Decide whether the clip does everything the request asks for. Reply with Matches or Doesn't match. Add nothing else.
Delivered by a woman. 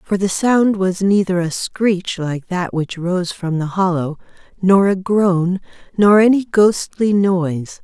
Matches